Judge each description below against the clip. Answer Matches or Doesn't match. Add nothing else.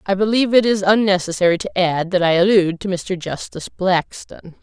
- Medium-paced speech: Matches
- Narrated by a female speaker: Matches